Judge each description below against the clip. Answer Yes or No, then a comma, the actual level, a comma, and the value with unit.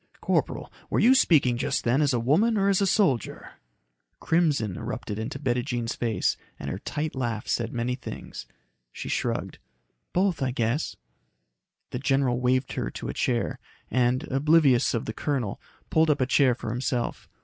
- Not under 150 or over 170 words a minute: Yes, average, 165 wpm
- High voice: No, low, 130 Hz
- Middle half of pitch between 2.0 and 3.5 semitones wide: No, average, 4.1 semitones